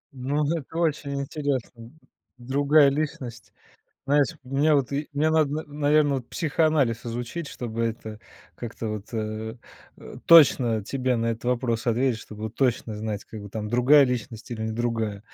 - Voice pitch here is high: No, low, 125 Hz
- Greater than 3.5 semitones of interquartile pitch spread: Yes, average, 4.2 semitones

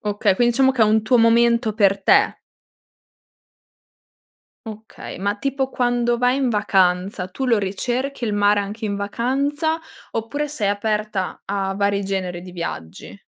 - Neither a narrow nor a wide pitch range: Yes, average, 3.4 semitones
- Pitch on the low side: No, high, 215 Hz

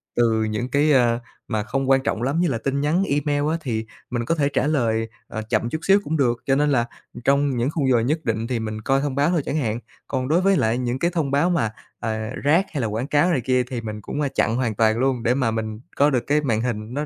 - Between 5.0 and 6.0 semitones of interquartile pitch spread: No, average, 4.2 semitones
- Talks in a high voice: No, low, 130 Hz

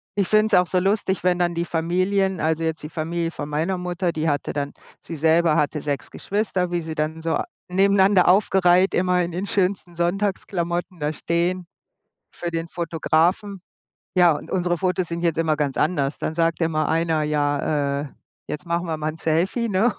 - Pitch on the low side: No, medium, 170 Hz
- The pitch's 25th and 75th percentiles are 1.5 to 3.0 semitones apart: Yes, narrow, 2.5 semitones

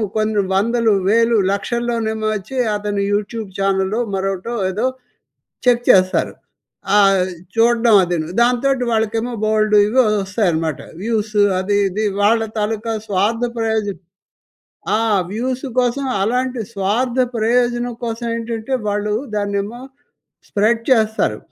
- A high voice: Yes, high, 220 Hz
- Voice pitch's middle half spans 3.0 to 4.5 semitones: No, narrow, 2.6 semitones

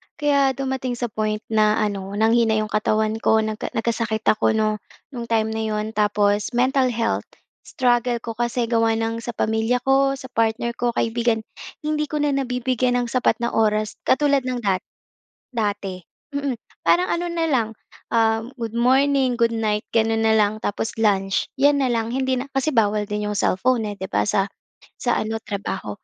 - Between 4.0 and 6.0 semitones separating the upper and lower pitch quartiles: No, average, 2.9 semitones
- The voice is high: Yes, high, 230 Hz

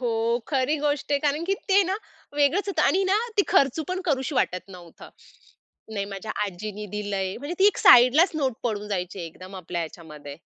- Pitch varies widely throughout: Yes, wide, 7.5 semitones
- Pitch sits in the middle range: No, high, 240 Hz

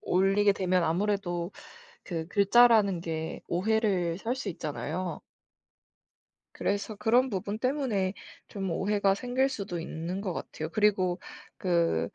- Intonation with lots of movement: No, average, 3.3 semitones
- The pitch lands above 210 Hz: No, high, 195 Hz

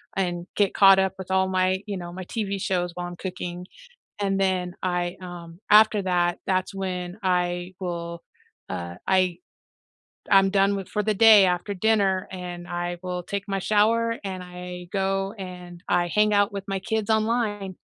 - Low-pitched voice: No, medium, 185 Hz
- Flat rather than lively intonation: Yes, narrow, 2.1 semitones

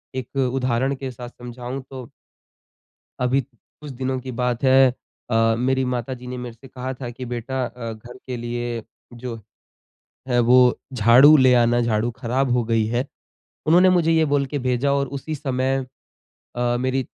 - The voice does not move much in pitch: Yes, narrow, 1.8 semitones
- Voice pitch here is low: Yes, low, 125 Hz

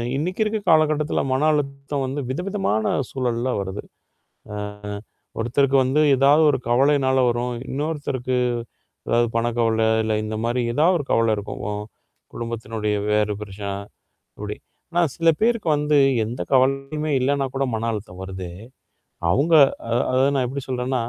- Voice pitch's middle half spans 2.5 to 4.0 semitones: No, average, 4.4 semitones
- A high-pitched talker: No, low, 130 Hz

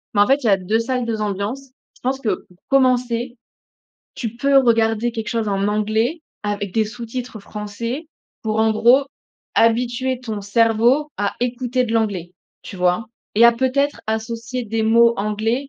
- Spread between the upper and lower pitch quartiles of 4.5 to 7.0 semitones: No, average, 2.8 semitones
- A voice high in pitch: Yes, high, 230 Hz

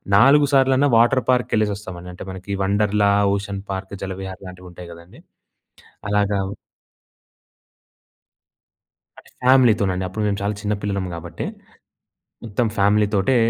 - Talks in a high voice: No, low, 100 Hz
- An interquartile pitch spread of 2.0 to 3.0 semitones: Yes, narrow, 2.4 semitones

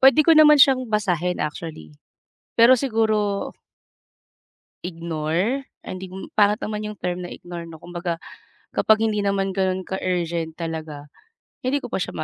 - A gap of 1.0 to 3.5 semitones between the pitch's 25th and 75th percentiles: No, average, 4.2 semitones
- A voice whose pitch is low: No, high, 190 Hz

